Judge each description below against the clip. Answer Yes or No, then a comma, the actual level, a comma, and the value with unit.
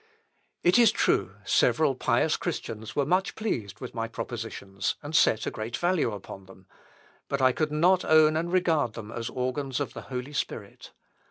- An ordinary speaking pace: Yes, average, 180 wpm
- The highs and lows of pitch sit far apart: Yes, wide, 6.1 semitones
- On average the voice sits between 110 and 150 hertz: Yes, low, 135 Hz